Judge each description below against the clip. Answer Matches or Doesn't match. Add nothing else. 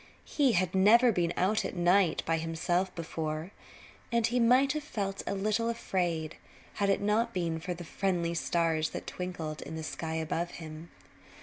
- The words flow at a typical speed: Matches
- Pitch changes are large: Doesn't match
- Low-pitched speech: Doesn't match